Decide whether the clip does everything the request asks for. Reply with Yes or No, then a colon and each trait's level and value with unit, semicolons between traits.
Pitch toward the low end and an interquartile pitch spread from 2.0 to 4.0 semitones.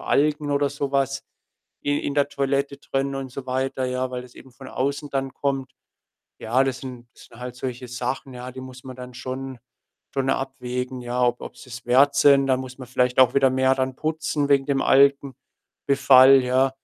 No: low, 130 Hz; narrow, 1.4 semitones